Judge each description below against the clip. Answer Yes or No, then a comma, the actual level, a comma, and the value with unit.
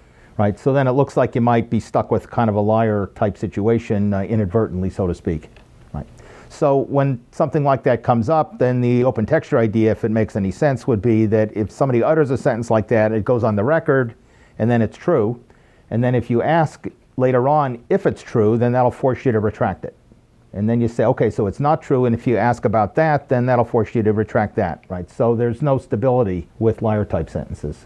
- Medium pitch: No, low, 115 Hz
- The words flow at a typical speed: No, fast, 230 wpm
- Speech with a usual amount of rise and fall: Yes, average, 3.2 semitones